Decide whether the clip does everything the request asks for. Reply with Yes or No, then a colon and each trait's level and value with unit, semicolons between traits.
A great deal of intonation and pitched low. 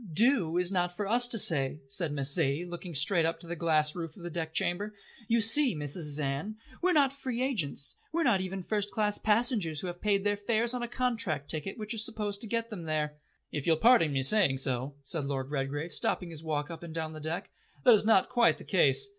No: wide, 6.2 semitones; medium, 175 Hz